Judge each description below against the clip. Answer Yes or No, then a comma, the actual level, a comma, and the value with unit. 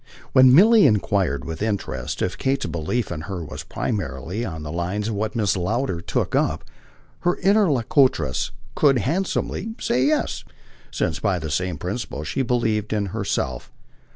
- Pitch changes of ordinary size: No, wide, 7.0 semitones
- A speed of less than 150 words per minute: No, average, 155 wpm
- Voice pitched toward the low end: Yes, low, 105 Hz